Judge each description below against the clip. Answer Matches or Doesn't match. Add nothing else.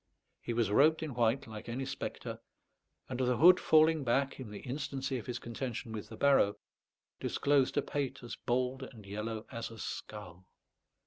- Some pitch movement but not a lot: Matches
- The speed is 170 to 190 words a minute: Matches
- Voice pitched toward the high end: Doesn't match